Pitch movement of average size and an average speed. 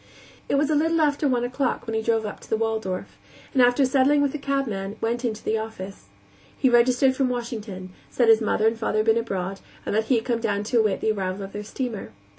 No: average, 3.4 semitones; fast, 235 wpm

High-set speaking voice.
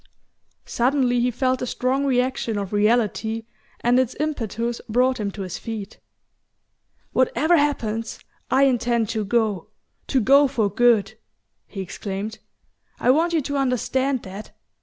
Yes: high, 240 Hz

